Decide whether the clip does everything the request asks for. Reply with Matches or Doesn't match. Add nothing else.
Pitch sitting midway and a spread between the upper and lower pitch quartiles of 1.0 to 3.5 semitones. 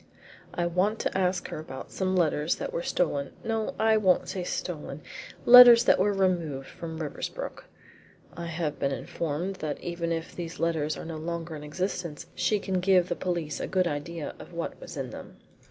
Matches